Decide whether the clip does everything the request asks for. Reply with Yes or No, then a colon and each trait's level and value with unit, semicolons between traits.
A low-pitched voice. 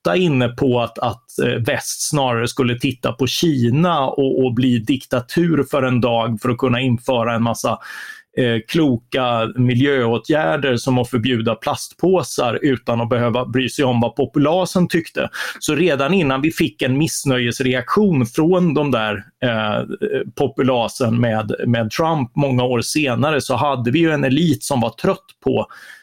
Yes: low, 130 Hz